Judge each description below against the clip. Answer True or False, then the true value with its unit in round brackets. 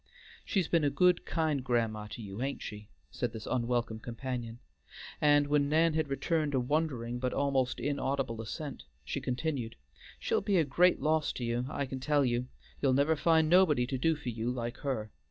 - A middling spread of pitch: True (4.0 semitones)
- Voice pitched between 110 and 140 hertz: True (135 Hz)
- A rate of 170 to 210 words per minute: True (190 wpm)